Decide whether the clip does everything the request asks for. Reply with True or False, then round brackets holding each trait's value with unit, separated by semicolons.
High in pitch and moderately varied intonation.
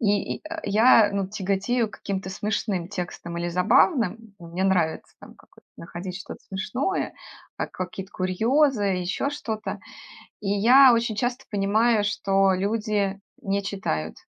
True (200 Hz; 3.1 semitones)